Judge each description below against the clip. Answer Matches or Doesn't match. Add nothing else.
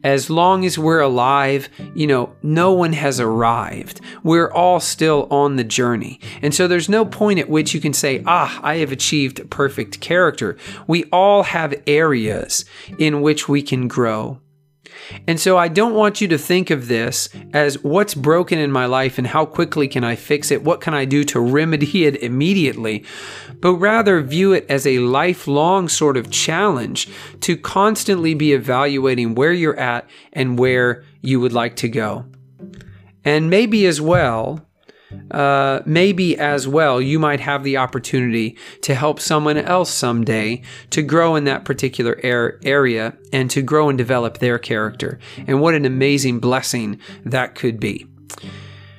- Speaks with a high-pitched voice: Doesn't match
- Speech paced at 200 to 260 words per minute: Doesn't match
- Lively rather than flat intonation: Doesn't match